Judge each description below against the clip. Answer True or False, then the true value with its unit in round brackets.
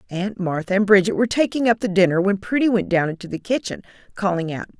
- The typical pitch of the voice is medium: False (195 Hz)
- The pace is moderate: False (225 wpm)